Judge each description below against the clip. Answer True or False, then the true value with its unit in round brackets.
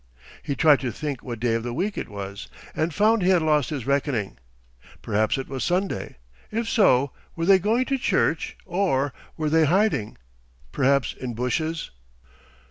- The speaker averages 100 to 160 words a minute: False (170 wpm)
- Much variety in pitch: True (6.8 semitones)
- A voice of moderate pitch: True (145 Hz)